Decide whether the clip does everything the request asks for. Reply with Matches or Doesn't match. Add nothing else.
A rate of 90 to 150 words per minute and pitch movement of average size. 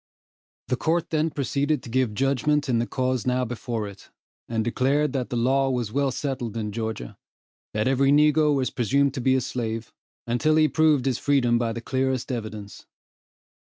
Doesn't match